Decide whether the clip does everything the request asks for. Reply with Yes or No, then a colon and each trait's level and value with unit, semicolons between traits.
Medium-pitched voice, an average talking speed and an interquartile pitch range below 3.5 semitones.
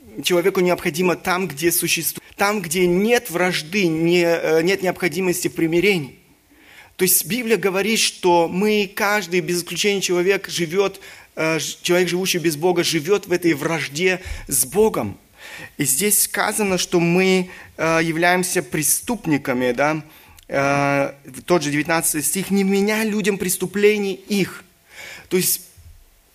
Yes: medium, 180 Hz; average, 120 wpm; average, 2.9 semitones